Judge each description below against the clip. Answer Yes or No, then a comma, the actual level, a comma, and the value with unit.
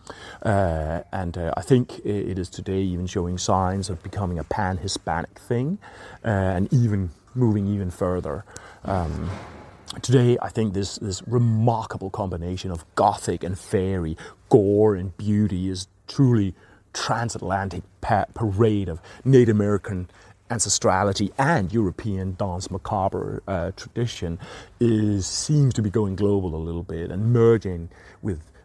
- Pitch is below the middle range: Yes, low, 100 Hz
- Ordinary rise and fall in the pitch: Yes, average, 3.2 semitones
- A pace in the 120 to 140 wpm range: Yes, slow, 135 wpm